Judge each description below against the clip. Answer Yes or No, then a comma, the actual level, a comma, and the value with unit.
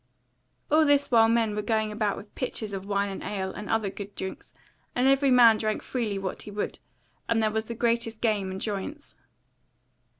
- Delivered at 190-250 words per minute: Yes, average, 195 wpm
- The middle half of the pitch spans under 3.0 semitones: Yes, narrow, 2.5 semitones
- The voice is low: No, high, 220 Hz